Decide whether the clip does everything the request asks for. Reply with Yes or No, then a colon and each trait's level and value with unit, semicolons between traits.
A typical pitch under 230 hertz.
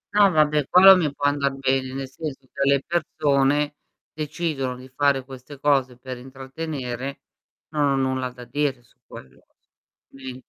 Yes: medium, 140 Hz